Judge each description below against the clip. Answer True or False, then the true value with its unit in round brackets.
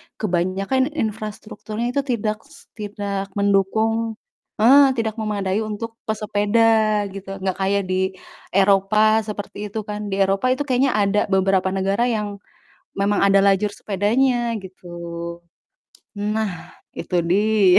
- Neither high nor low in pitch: False (210 Hz)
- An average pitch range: False (2.1 semitones)